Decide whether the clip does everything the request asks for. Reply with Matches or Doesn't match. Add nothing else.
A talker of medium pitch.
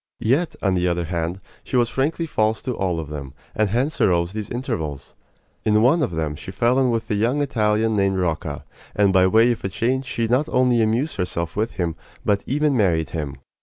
Doesn't match